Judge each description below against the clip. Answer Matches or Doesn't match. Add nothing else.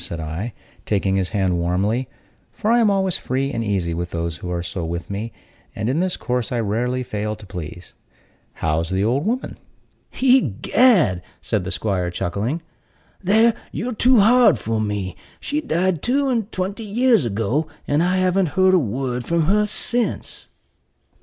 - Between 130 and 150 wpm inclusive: Doesn't match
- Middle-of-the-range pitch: Doesn't match